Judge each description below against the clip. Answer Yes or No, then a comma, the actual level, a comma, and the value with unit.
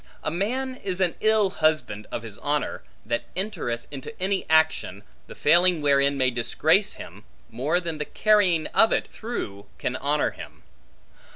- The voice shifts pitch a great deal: Yes, wide, 6.8 semitones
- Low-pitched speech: No, medium, 160 Hz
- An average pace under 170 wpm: Yes, average, 160 wpm